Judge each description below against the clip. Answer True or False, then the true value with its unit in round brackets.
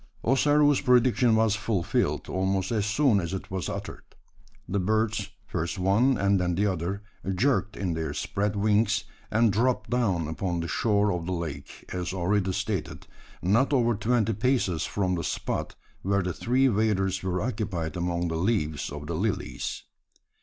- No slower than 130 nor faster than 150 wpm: False (160 wpm)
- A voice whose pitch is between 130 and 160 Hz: False (100 Hz)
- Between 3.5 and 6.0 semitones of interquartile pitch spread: True (3.9 semitones)